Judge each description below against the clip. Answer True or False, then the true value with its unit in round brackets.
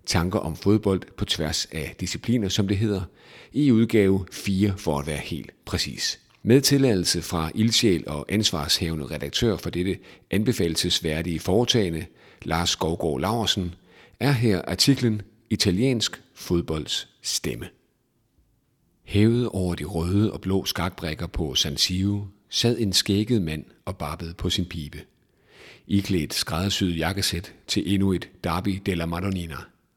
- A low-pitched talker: True (95 Hz)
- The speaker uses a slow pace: True (130 wpm)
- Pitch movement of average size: True (3.7 semitones)